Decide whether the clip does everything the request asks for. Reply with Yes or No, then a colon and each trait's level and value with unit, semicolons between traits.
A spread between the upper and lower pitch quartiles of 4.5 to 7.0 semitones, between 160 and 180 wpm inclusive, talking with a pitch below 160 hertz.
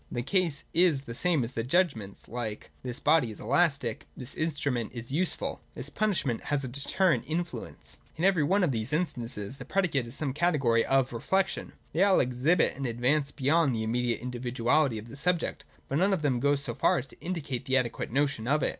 No: average, 5.1 semitones; average, 200 wpm; medium, 140 Hz